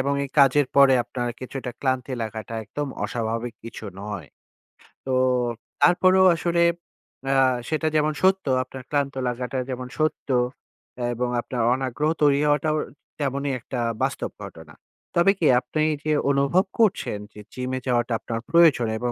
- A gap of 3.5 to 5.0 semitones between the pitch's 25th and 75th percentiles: Yes, average, 3.9 semitones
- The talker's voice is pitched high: No, low, 135 Hz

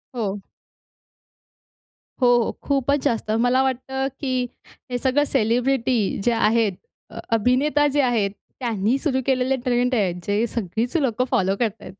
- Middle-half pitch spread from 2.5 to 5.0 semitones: Yes, average, 3.0 semitones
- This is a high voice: Yes, high, 245 Hz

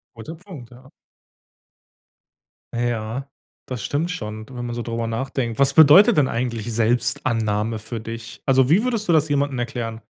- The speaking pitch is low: Yes, low, 120 Hz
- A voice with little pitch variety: No, average, 3.8 semitones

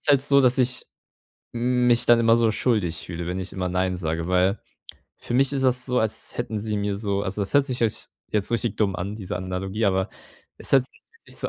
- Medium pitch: No, low, 105 Hz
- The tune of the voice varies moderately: Yes, average, 4.8 semitones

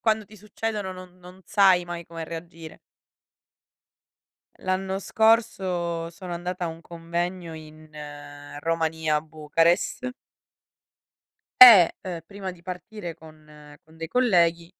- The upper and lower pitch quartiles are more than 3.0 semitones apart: No, narrow, 2.5 semitones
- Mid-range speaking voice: Yes, medium, 175 Hz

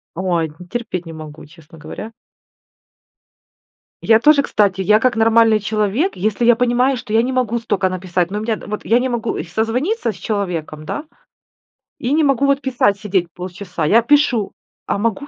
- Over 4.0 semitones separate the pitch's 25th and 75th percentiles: Yes, average, 4.7 semitones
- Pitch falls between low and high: No, high, 220 Hz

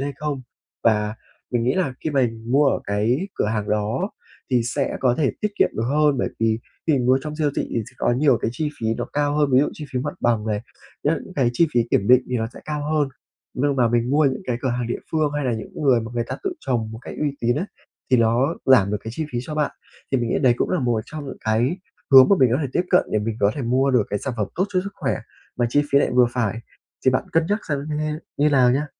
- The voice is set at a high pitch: No, low, 130 Hz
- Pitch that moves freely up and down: No, average, 4.0 semitones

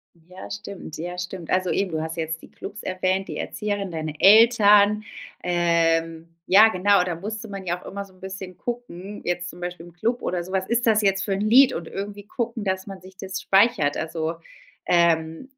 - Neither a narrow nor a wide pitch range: Yes, average, 3.2 semitones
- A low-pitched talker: No, high, 190 Hz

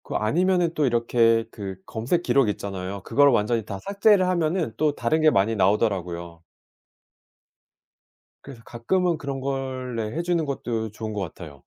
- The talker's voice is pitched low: Yes, low, 120 Hz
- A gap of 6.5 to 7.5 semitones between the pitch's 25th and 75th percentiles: Yes, wide, 7.0 semitones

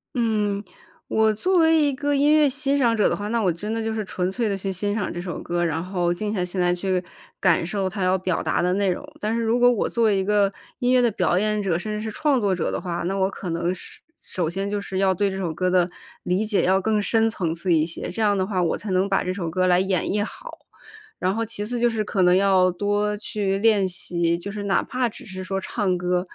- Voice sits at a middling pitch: No, high, 195 Hz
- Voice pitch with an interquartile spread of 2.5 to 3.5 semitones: Yes, average, 3.1 semitones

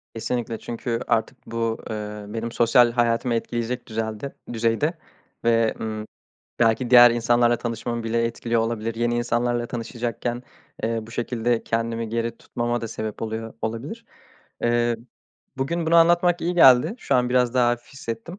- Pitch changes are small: Yes, narrow, 1.2 semitones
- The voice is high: No, low, 120 Hz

